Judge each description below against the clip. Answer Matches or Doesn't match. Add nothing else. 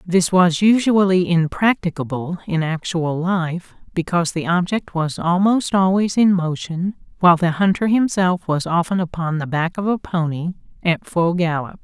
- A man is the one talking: Doesn't match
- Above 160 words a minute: Doesn't match